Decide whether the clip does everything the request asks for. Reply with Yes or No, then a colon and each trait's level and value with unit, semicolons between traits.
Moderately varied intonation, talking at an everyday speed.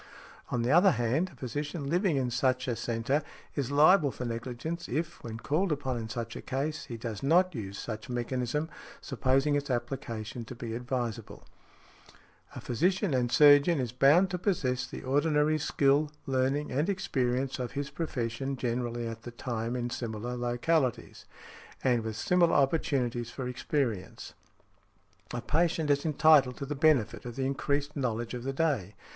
Yes: average, 3.7 semitones; average, 165 wpm